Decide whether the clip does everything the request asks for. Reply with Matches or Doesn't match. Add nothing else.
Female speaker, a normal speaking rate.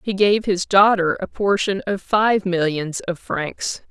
Matches